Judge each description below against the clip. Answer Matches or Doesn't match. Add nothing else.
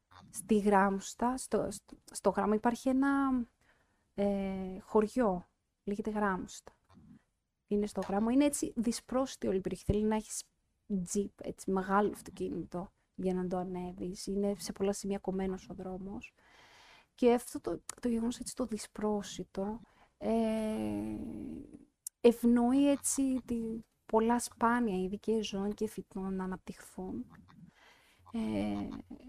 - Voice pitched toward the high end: Matches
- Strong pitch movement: Doesn't match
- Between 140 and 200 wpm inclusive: Doesn't match